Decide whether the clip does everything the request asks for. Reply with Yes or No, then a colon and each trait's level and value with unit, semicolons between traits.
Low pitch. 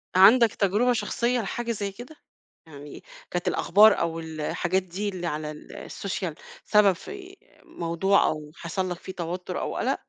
No: high, 190 Hz